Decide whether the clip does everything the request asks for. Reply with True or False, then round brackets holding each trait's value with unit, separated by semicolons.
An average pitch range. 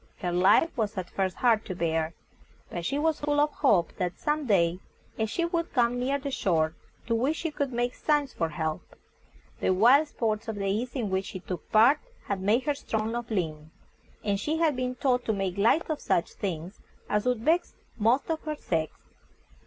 False (7.0 semitones)